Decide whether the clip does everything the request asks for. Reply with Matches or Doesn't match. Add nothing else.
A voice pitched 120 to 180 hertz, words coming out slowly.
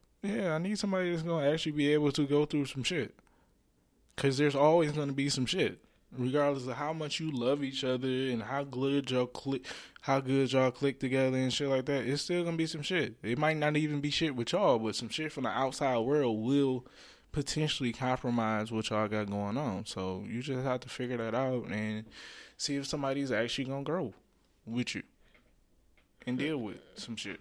Doesn't match